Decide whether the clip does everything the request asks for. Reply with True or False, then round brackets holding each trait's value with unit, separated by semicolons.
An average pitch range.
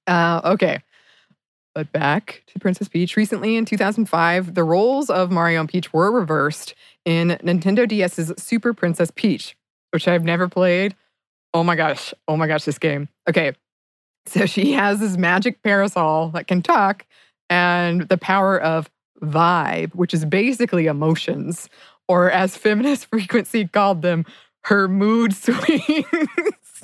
True (3.8 semitones)